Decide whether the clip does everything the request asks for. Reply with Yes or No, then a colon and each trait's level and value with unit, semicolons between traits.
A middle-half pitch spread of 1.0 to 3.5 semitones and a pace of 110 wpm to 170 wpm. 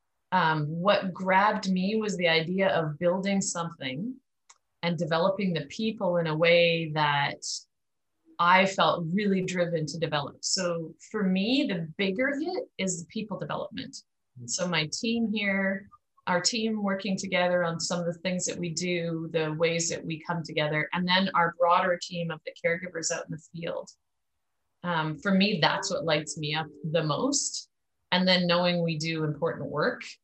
Yes: average, 3.2 semitones; average, 165 wpm